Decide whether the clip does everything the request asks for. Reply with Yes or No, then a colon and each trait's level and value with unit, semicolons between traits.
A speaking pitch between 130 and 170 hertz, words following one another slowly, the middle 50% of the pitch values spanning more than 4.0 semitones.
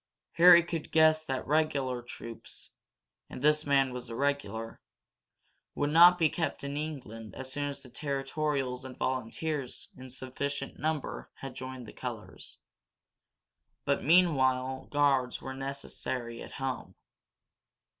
No: low, 135 Hz; slow, 130 wpm; average, 2.9 semitones